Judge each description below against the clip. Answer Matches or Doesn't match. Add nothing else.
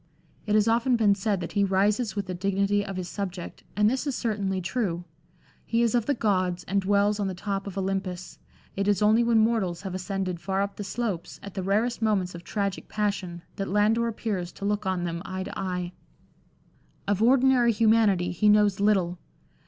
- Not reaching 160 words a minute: Doesn't match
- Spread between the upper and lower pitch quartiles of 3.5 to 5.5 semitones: Doesn't match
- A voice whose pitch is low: Doesn't match